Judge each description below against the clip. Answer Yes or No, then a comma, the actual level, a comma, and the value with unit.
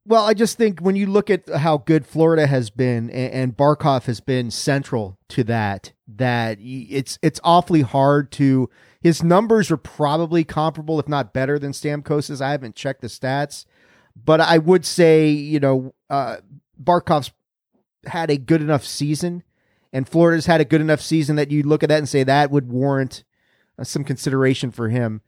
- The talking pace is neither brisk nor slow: Yes, average, 180 wpm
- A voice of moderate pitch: Yes, medium, 145 Hz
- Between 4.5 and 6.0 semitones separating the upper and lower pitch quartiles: No, average, 3.6 semitones